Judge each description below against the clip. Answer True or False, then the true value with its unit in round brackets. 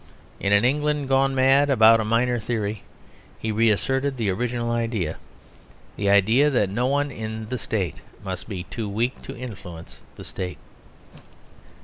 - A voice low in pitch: True (115 Hz)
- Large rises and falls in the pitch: False (4.2 semitones)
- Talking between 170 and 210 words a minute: False (150 wpm)